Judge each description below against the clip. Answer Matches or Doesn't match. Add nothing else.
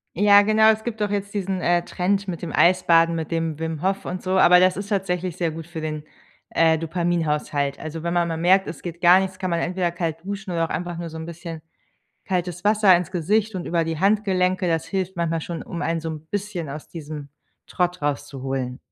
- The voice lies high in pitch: Doesn't match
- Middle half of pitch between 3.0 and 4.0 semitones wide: Doesn't match